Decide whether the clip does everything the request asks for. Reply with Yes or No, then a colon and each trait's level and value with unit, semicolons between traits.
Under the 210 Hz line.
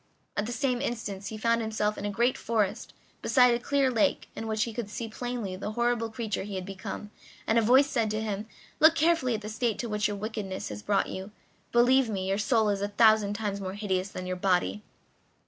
No: high, 215 Hz